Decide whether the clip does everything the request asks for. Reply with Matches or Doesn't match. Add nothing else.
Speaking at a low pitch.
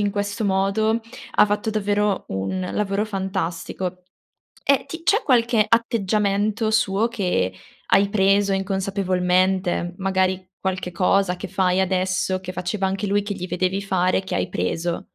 Doesn't match